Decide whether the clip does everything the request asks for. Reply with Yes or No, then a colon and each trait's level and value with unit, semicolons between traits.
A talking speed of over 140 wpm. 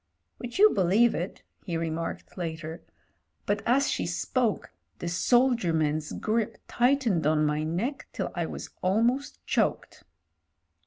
No: slow, 135 wpm